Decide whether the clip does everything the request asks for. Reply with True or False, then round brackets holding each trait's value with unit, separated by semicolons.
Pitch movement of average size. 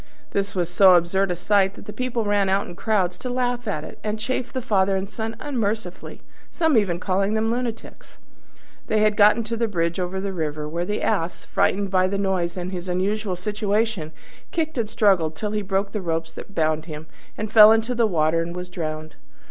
True (3.6 semitones)